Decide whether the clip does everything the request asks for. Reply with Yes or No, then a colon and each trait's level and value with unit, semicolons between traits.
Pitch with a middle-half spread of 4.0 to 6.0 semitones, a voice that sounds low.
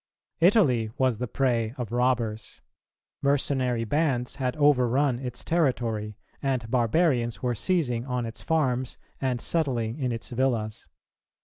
No: average, 2.8 semitones; low, 125 Hz